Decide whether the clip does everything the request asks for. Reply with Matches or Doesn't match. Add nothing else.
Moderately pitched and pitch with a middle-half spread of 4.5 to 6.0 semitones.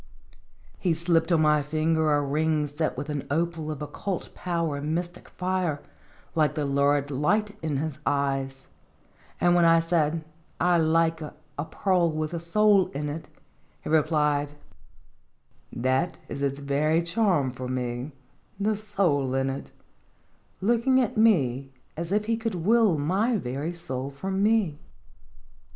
Doesn't match